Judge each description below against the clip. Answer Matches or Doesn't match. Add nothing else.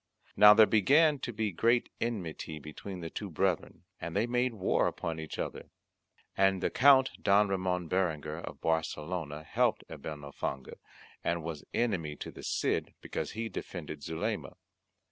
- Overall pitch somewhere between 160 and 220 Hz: Doesn't match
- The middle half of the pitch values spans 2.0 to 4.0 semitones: Doesn't match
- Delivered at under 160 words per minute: Matches